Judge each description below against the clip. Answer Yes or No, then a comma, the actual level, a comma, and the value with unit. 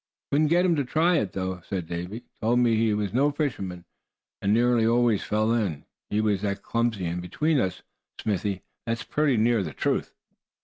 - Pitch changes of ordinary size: Yes, average, 4.2 semitones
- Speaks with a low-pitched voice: Yes, low, 110 Hz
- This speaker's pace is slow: No, average, 185 wpm